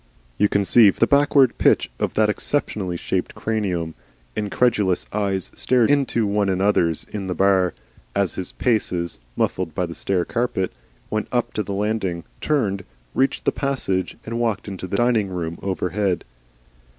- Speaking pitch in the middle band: No, low, 100 Hz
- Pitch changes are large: No, average, 3.6 semitones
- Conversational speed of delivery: Yes, average, 150 wpm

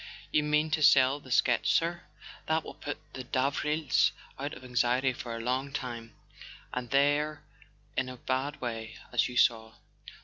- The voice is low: Yes, low, 130 Hz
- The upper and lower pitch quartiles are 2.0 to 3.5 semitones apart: Yes, average, 3.1 semitones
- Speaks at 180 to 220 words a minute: No, average, 165 wpm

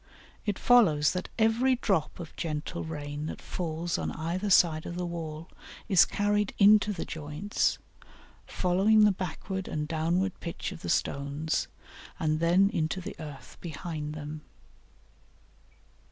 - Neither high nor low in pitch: Yes, medium, 170 Hz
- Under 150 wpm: Yes, average, 140 wpm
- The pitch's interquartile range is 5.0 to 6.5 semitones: No, average, 3.9 semitones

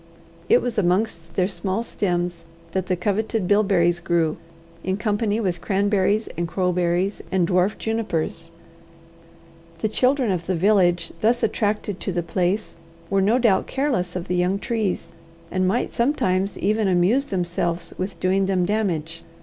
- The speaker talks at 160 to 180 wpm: No, average, 150 wpm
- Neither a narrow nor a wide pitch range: Yes, average, 3.2 semitones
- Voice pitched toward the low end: No, high, 190 Hz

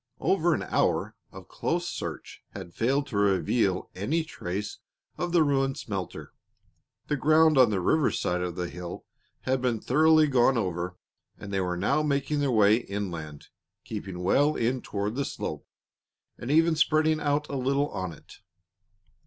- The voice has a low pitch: Yes, low, 120 Hz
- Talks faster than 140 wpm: Yes, average, 160 wpm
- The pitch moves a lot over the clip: Yes, wide, 7.4 semitones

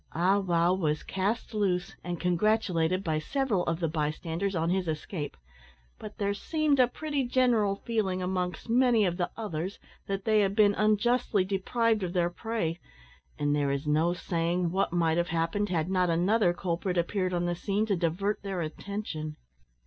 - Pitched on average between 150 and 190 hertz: Yes, medium, 185 Hz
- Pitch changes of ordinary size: Yes, average, 3.7 semitones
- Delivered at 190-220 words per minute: No, average, 170 wpm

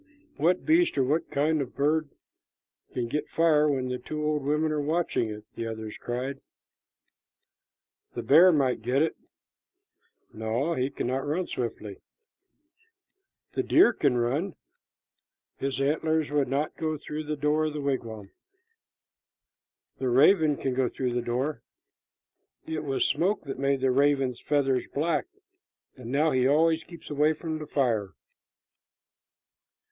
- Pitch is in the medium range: Yes, medium, 145 Hz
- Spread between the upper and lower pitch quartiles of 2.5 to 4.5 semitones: Yes, average, 3.5 semitones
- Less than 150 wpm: Yes, average, 140 wpm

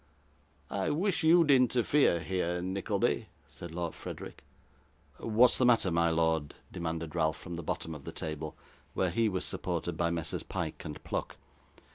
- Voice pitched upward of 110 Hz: No, very low, 85 Hz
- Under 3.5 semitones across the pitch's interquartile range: No, wide, 5.6 semitones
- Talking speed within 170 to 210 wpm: No, average, 160 wpm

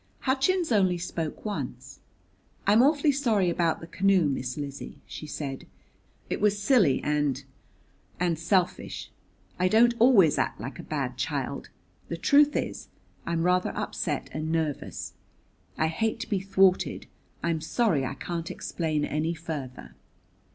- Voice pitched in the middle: Yes, medium, 175 Hz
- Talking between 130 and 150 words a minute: Yes, average, 140 wpm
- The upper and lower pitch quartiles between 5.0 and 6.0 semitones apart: Yes, wide, 5.4 semitones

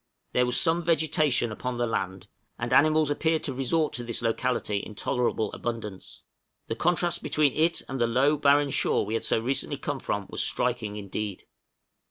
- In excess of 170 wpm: Yes, average, 180 wpm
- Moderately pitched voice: No, low, 125 Hz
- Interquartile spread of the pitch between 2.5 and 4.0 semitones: No, average, 5.0 semitones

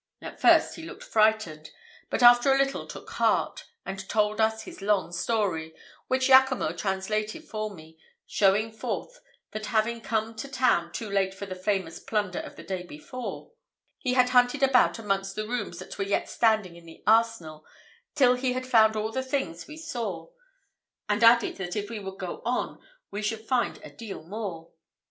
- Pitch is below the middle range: No, high, 215 Hz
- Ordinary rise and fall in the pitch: Yes, average, 4.1 semitones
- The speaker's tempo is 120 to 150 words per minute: No, average, 180 wpm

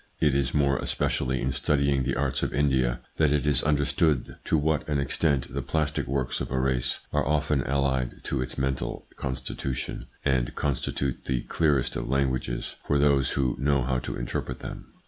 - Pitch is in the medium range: No, very low, 70 Hz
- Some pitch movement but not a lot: No, narrow, 2.0 semitones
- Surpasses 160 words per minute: Yes, average, 180 wpm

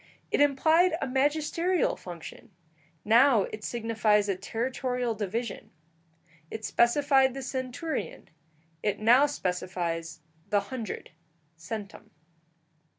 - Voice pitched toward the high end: Yes, high, 235 Hz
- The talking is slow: Yes, slow, 95 wpm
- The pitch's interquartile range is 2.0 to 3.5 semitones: No, average, 4.7 semitones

